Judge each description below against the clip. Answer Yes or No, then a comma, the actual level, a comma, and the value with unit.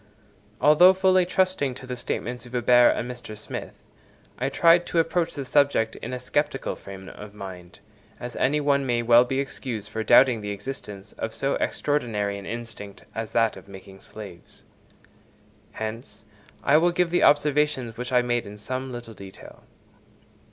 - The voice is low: Yes, low, 120 Hz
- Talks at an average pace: Yes, average, 165 wpm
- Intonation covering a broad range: No, average, 4.8 semitones